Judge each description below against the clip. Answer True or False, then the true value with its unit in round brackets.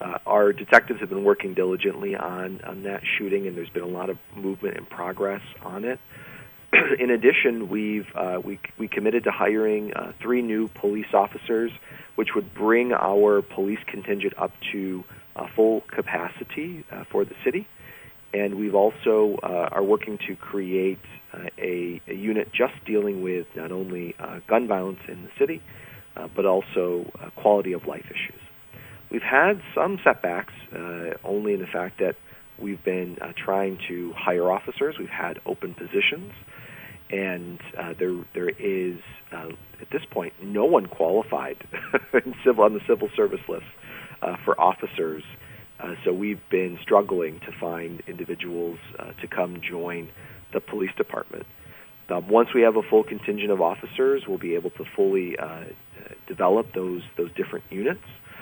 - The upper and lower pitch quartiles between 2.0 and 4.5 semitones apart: True (3.1 semitones)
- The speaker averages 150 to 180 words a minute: True (165 wpm)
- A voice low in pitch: True (100 Hz)